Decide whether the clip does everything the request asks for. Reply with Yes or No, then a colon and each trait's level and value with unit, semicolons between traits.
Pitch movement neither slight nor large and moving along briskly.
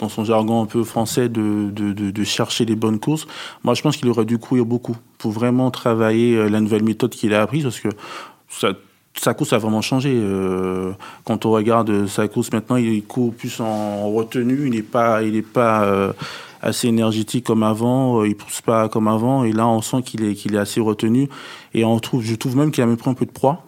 No: narrow, 2.3 semitones; fast, 230 wpm